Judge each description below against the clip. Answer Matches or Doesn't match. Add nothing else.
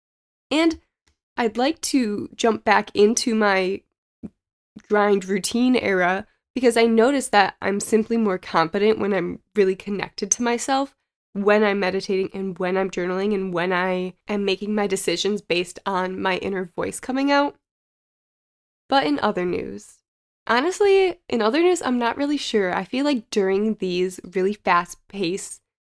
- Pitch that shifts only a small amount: Doesn't match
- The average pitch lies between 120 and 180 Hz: Doesn't match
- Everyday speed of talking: Matches